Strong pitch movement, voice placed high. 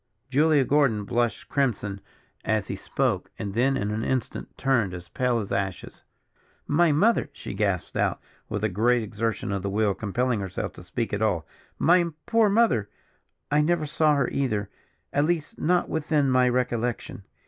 No: wide, 6.0 semitones; low, 120 Hz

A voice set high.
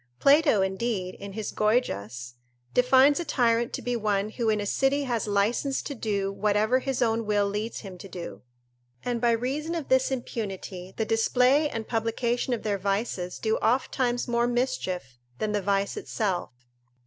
Yes: high, 225 Hz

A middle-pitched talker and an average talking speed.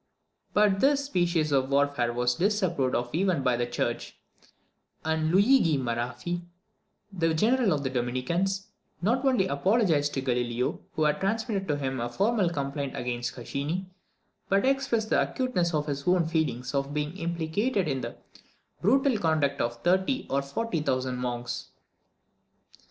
Yes: medium, 155 Hz; average, 145 wpm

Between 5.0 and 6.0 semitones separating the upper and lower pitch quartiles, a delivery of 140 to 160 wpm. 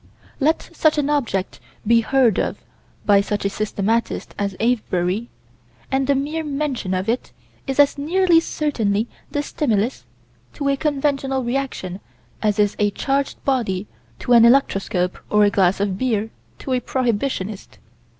Yes: wide, 5.4 semitones; average, 150 wpm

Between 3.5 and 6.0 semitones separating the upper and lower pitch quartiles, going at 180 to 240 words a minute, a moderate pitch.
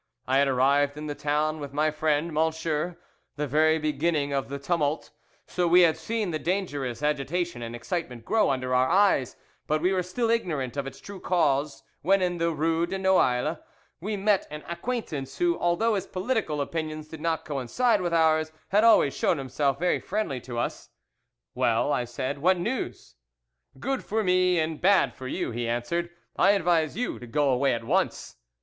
Yes: average, 4.6 semitones; average, 185 wpm; medium, 155 Hz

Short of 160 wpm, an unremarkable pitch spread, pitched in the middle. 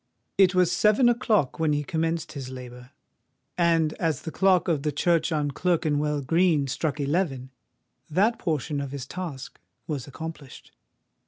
Yes: average, 150 wpm; average, 3.8 semitones; medium, 155 Hz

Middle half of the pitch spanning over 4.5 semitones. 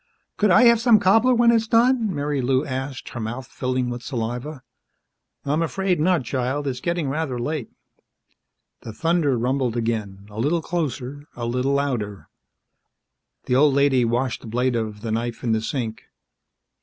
Yes: average, 5.1 semitones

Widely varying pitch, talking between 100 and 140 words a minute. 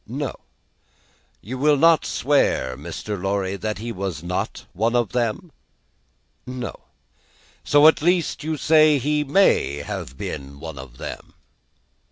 Yes: wide, 8.5 semitones; slow, 135 wpm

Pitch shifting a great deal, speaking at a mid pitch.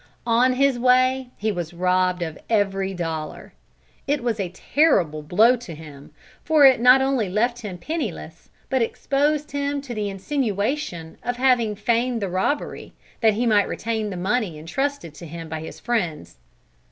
No: wide, 6.1 semitones; high, 220 Hz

